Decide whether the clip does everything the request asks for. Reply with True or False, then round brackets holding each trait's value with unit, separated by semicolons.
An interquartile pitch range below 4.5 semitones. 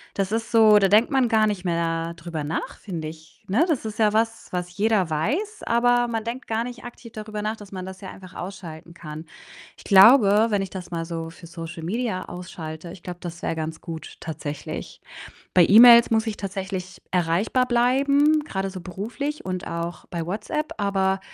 False (4.9 semitones)